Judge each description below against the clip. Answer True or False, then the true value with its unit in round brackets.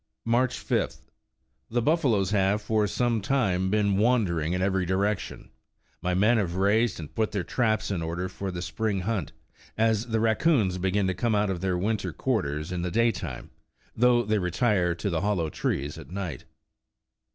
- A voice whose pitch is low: True (100 Hz)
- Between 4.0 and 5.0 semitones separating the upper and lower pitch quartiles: False (3.6 semitones)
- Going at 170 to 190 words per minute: True (180 wpm)